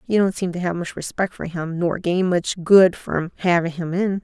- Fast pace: Yes, fast, 240 wpm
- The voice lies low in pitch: No, medium, 175 Hz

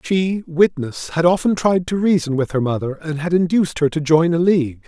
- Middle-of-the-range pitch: Yes, medium, 165 Hz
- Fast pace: Yes, fast, 220 wpm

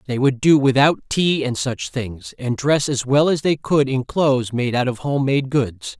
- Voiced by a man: Yes, male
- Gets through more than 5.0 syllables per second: No, 4.4 syllables/s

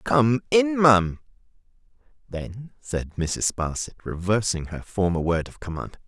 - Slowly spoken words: Yes, slow, 130 wpm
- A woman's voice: No, male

